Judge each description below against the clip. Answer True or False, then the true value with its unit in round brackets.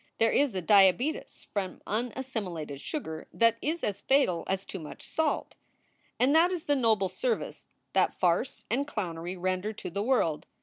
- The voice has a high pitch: True (215 Hz)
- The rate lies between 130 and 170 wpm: True (165 wpm)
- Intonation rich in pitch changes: True (6.7 semitones)